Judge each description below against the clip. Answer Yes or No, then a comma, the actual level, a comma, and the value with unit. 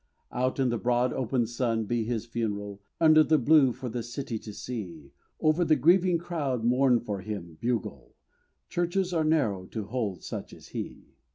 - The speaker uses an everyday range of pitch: No, wide, 5.7 semitones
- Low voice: Yes, low, 120 Hz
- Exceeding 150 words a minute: Yes, average, 175 wpm